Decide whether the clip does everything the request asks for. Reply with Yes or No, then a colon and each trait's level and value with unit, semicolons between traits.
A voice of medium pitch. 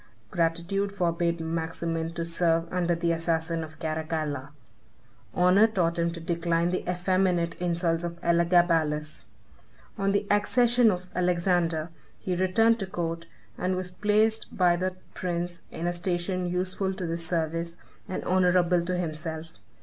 Yes: medium, 175 Hz